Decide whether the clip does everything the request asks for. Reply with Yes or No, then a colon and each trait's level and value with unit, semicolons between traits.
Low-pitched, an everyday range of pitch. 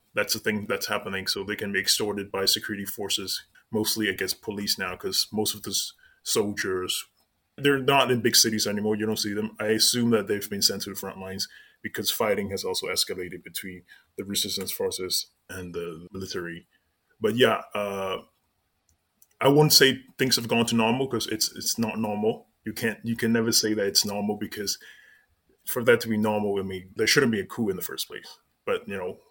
Yes: low, 105 Hz; average, 3.2 semitones